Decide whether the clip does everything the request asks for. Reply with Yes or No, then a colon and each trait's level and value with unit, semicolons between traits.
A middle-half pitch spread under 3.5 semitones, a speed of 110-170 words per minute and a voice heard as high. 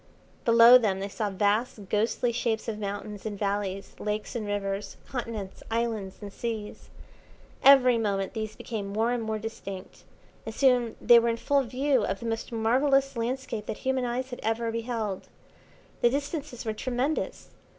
Yes: average, 2.9 semitones; average, 160 wpm; high, 225 Hz